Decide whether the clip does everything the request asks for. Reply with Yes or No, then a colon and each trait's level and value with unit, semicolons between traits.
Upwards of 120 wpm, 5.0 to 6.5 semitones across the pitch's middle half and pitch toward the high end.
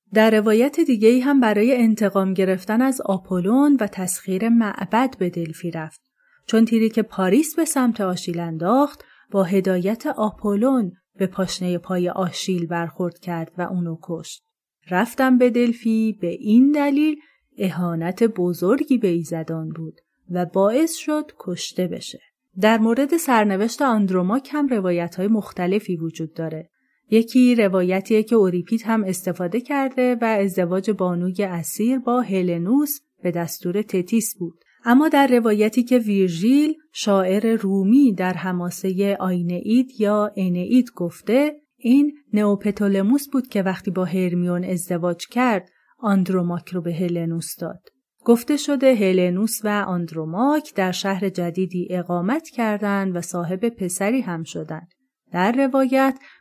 Yes: average, 130 wpm; average, 5.3 semitones; high, 200 Hz